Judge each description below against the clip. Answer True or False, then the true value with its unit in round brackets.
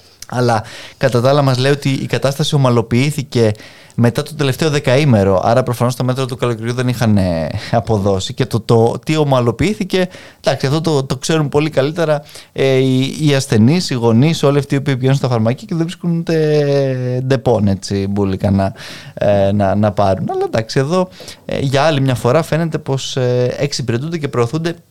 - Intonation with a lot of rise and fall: False (3.9 semitones)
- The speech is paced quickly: True (175 wpm)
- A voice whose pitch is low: True (130 Hz)